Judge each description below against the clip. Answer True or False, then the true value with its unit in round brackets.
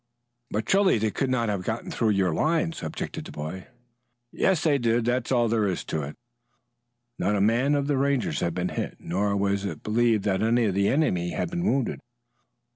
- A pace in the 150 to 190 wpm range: False (200 wpm)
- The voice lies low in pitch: True (110 Hz)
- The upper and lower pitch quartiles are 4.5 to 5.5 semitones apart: True (5.2 semitones)